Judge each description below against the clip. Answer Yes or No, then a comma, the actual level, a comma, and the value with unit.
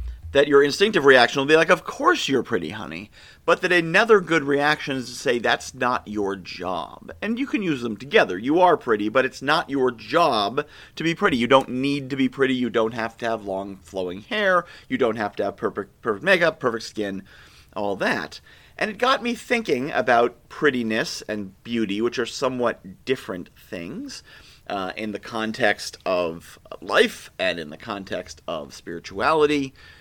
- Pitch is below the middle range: Yes, low, 130 Hz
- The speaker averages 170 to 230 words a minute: Yes, average, 185 wpm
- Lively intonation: Yes, wide, 6.9 semitones